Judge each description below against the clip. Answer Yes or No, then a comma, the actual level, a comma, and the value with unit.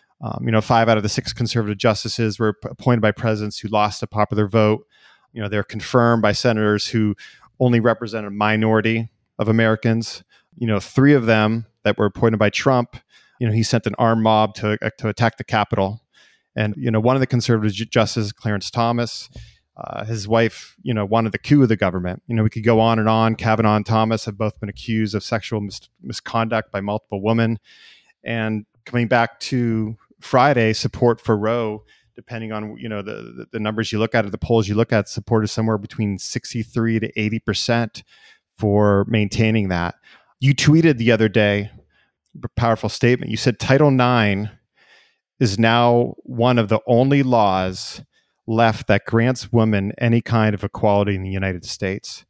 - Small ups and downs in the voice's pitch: Yes, narrow, 1.7 semitones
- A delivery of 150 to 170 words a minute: No, average, 190 wpm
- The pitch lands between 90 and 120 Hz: Yes, low, 110 Hz